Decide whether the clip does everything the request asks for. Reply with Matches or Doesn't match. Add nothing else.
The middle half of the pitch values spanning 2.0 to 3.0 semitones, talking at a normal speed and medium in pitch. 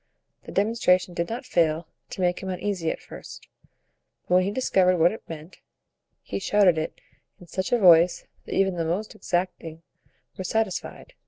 Matches